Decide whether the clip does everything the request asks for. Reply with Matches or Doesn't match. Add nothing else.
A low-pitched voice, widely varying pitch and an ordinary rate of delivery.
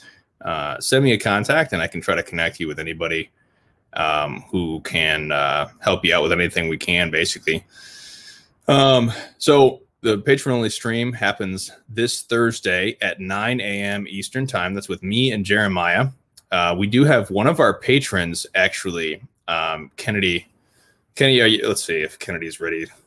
Matches